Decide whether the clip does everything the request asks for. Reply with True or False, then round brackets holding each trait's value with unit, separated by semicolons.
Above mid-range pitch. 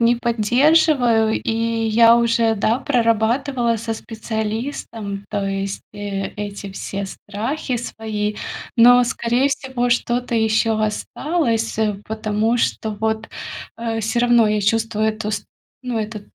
True (225 Hz)